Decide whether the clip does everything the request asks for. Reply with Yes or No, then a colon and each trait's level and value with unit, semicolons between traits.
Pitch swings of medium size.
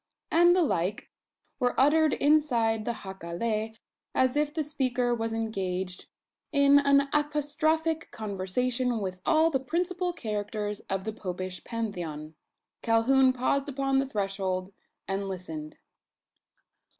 No: wide, 6.6 semitones